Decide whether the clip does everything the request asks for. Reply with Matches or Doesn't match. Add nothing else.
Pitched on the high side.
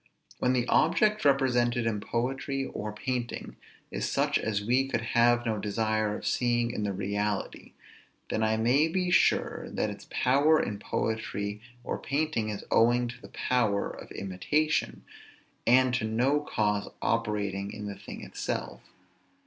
Doesn't match